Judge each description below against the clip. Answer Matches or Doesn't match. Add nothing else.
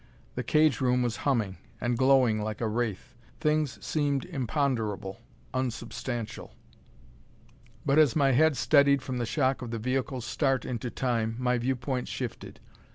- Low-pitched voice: Matches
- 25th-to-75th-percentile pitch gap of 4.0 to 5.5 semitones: Doesn't match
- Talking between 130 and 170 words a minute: Matches